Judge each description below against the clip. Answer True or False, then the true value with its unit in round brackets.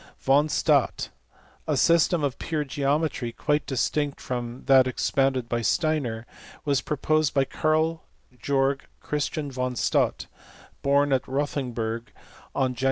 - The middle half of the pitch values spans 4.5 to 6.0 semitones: False (2.8 semitones)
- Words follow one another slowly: True (125 wpm)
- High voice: False (140 Hz)